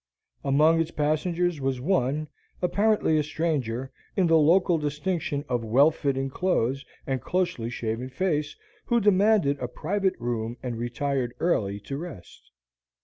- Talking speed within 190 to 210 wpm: No, average, 140 wpm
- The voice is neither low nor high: Yes, medium, 145 Hz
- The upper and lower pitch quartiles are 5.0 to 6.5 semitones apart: Yes, wide, 5.5 semitones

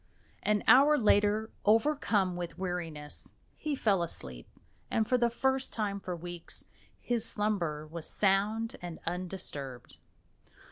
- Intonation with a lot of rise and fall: No, average, 4.5 semitones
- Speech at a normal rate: No, slow, 125 wpm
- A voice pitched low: No, high, 200 Hz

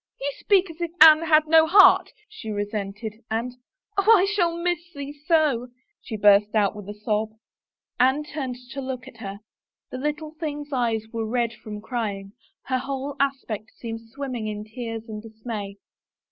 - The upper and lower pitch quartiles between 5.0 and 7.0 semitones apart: Yes, wide, 5.5 semitones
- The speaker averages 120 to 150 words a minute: No, average, 180 wpm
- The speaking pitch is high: Yes, high, 245 Hz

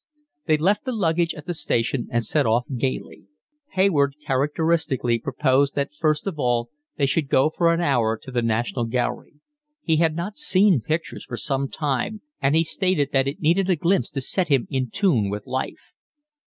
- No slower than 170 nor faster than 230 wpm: Yes, average, 185 wpm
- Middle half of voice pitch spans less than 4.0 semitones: No, average, 4.8 semitones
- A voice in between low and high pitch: Yes, medium, 145 Hz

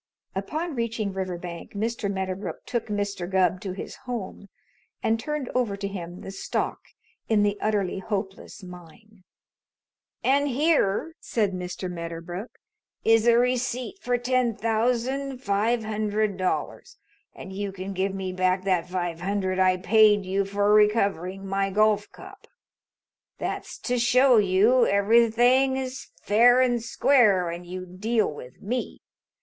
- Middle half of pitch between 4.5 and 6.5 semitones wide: No, average, 4.0 semitones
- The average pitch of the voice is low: No, high, 205 Hz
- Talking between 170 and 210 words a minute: No, average, 140 wpm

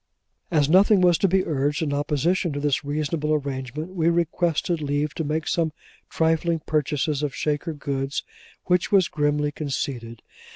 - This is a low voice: No, medium, 150 Hz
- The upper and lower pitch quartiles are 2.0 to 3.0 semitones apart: Yes, average, 2.7 semitones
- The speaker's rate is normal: Yes, average, 155 wpm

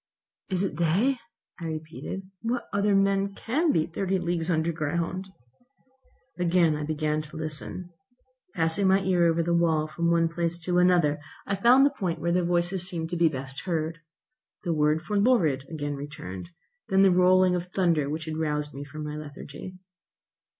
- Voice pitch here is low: No, medium, 170 Hz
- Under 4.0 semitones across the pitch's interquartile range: Yes, average, 3.1 semitones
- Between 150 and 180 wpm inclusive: Yes, average, 170 wpm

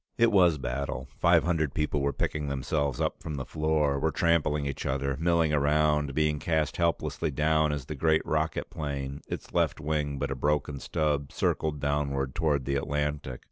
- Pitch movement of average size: No, narrow, 1.9 semitones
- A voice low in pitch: Yes, very low, 75 Hz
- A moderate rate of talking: Yes, average, 180 wpm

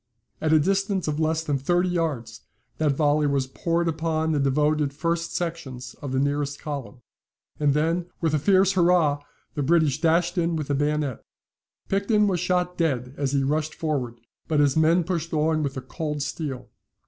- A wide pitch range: No, average, 3.0 semitones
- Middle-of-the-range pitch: Yes, medium, 155 Hz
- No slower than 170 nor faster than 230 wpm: Yes, average, 180 wpm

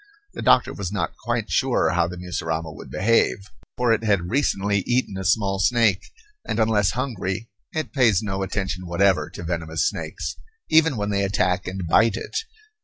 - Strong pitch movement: No, average, 4.1 semitones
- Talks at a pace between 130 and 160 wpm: No, average, 175 wpm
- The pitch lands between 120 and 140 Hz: No, low, 100 Hz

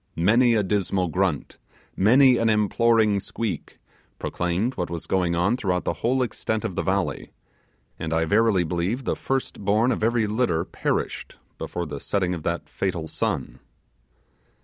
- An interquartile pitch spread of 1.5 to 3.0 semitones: No, average, 4.7 semitones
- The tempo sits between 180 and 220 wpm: No, average, 155 wpm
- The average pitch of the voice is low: Yes, low, 100 Hz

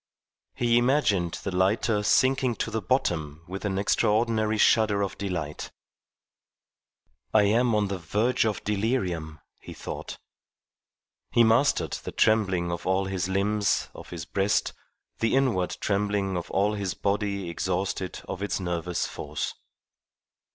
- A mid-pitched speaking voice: No, low, 100 Hz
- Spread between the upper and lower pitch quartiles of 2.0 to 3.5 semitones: Yes, average, 3.1 semitones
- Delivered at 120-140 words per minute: Yes, slow, 135 wpm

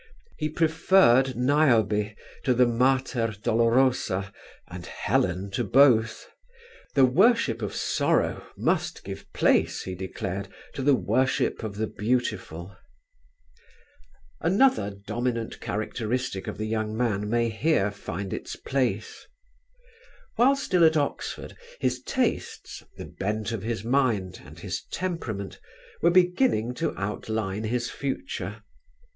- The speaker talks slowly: Yes, slow, 120 wpm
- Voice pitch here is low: Yes, low, 115 Hz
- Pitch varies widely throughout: No, average, 4.6 semitones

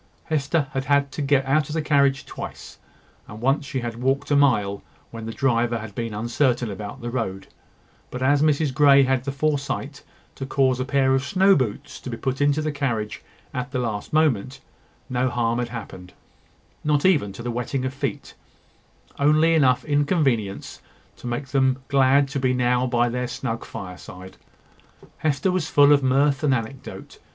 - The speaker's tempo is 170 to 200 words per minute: Yes, average, 180 wpm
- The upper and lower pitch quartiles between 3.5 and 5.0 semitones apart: No, average, 3.0 semitones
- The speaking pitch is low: Yes, low, 130 Hz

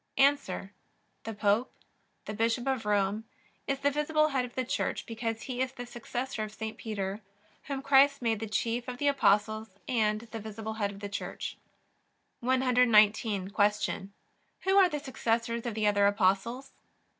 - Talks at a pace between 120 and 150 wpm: No, average, 165 wpm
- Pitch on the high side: Yes, high, 225 Hz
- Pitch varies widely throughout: No, average, 3.5 semitones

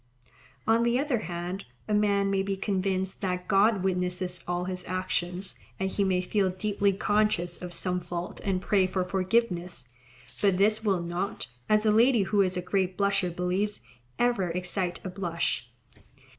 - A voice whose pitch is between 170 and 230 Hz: Yes, high, 190 Hz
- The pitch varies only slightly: Yes, narrow, 2.1 semitones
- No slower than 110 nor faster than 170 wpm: Yes, average, 165 wpm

